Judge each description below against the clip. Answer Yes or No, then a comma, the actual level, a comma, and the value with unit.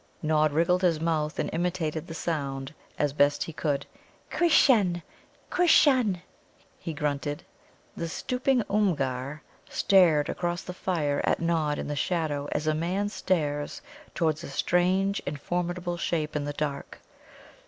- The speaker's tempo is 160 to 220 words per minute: No, average, 140 wpm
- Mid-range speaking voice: Yes, medium, 165 Hz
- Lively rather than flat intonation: No, average, 3.4 semitones